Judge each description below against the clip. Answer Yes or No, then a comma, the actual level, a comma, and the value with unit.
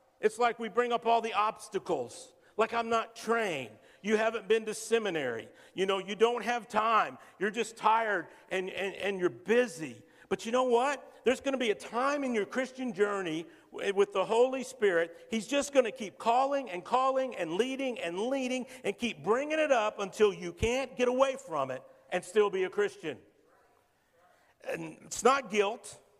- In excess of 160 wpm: Yes, average, 190 wpm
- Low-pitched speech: No, high, 225 Hz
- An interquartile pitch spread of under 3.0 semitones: No, average, 4.3 semitones